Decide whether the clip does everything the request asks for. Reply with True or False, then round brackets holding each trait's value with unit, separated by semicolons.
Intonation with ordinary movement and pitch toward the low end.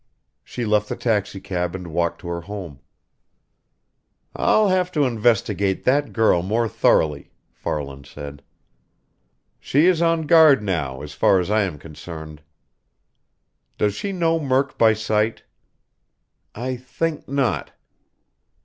False (7.8 semitones; 105 Hz)